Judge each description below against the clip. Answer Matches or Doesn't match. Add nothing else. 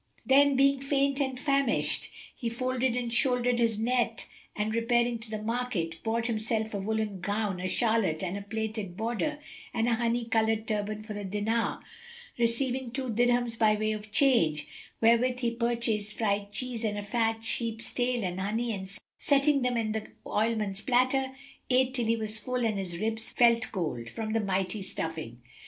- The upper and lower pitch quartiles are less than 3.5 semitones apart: Matches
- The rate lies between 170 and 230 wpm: Matches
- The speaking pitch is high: Matches